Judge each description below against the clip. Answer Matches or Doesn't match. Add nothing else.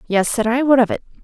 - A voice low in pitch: Doesn't match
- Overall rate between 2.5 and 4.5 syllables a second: Doesn't match